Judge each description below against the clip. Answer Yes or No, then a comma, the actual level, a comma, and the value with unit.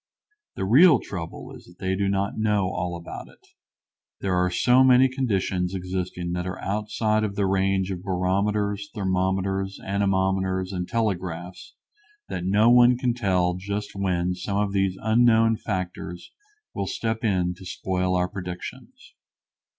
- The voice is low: Yes, very low, 95 Hz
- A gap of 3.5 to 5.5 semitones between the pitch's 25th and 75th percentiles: No, narrow, 2.4 semitones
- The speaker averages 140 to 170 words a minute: Yes, average, 150 wpm